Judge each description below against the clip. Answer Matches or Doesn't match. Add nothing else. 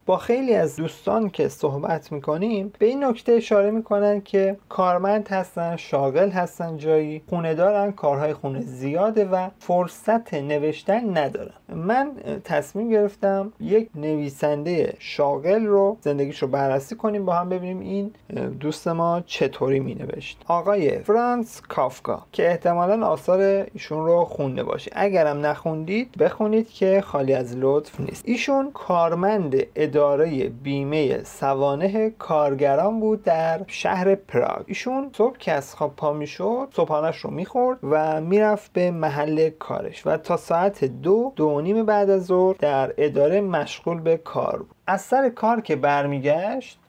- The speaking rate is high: Doesn't match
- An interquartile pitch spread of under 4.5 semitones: Doesn't match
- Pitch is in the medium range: Matches